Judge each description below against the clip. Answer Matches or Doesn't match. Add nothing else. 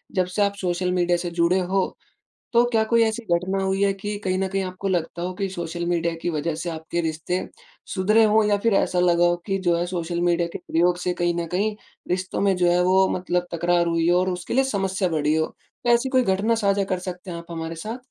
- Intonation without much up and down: Matches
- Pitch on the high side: Doesn't match